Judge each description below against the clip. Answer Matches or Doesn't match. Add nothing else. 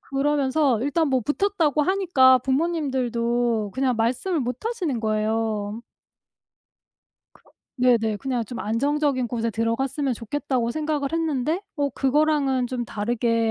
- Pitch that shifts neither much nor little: Matches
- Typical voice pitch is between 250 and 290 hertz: Matches